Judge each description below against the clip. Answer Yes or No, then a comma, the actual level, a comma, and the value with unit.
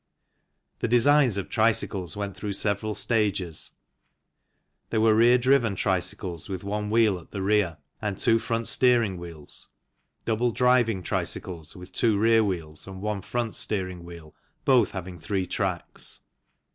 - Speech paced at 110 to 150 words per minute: Yes, average, 145 wpm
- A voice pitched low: Yes, low, 100 Hz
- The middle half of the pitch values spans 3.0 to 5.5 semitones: Yes, average, 3.7 semitones